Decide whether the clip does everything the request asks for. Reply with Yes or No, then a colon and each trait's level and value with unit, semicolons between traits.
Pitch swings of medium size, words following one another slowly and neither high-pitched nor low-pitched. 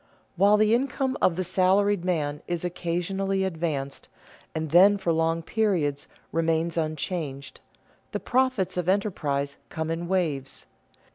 Yes: average, 3.5 semitones; slow, 130 wpm; medium, 175 Hz